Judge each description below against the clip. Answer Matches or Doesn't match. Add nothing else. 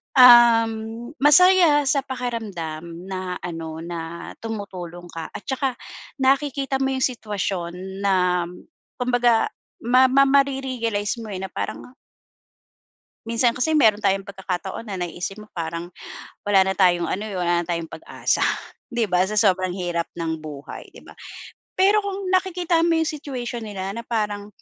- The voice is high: Matches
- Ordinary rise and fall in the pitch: Doesn't match